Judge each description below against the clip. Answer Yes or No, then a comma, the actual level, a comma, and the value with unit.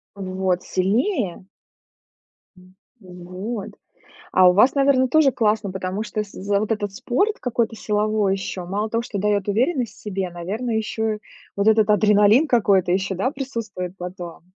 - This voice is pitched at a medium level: No, high, 210 Hz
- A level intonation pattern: No, average, 3.4 semitones